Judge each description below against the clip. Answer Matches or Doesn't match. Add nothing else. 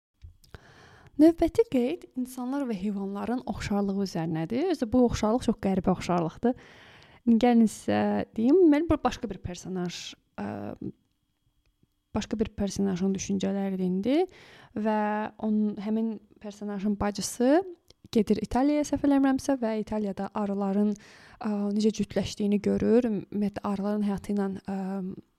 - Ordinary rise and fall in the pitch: Matches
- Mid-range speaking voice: Doesn't match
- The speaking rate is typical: Matches